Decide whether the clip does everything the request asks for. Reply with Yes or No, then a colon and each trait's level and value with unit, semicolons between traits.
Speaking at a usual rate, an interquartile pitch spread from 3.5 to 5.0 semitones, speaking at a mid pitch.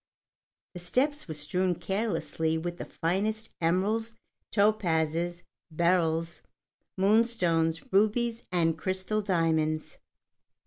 No: slow, 90 wpm; average, 4.6 semitones; medium, 180 Hz